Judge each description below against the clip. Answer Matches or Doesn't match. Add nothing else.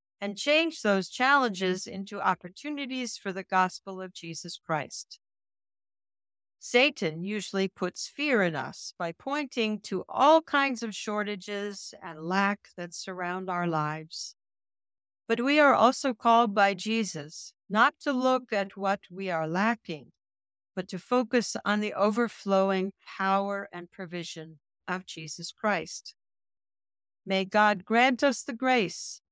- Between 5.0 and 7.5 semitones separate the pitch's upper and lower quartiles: Matches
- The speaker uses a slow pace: Matches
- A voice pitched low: Doesn't match